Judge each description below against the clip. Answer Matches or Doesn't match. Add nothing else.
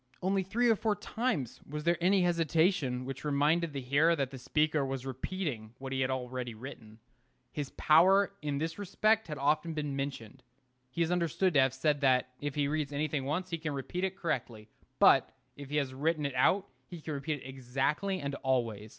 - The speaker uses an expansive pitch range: Doesn't match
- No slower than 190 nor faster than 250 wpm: Matches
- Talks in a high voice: Doesn't match